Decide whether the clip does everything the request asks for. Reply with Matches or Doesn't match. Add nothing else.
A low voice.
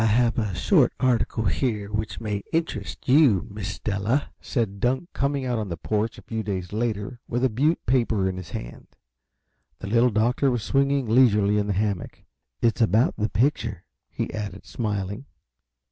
Matches